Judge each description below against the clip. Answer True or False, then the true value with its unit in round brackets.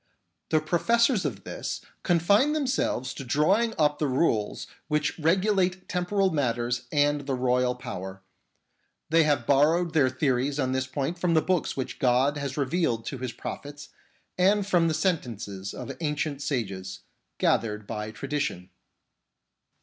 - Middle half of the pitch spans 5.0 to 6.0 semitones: True (5.3 semitones)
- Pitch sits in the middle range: True (145 Hz)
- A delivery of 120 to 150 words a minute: True (140 wpm)